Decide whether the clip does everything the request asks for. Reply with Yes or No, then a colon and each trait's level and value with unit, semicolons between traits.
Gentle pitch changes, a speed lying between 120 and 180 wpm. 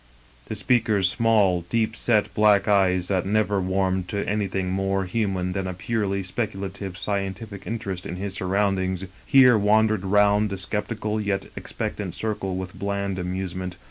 Yes: narrow, 2.1 semitones; average, 145 wpm